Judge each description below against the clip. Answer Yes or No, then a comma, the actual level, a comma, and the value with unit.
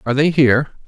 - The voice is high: No, low, 135 Hz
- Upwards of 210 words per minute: No, fast, 205 wpm